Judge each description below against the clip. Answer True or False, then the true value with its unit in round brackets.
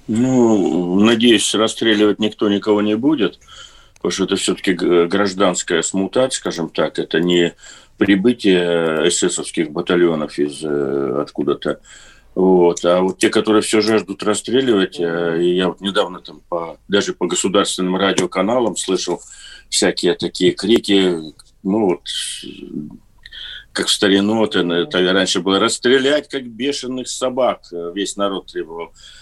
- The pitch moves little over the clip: False (3.8 semitones)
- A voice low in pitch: True (95 Hz)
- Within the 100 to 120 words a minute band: True (115 wpm)